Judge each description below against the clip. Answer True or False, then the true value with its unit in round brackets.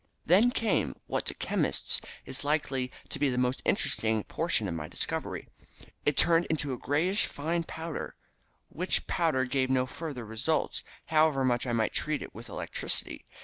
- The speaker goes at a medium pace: True (165 wpm)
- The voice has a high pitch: False (140 Hz)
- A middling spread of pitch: True (4.3 semitones)